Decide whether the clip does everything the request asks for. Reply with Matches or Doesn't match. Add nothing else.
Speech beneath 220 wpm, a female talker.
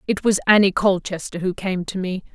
Matches